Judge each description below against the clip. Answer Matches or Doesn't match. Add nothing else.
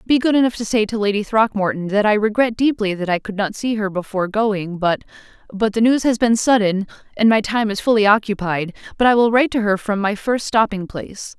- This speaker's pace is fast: Matches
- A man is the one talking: Doesn't match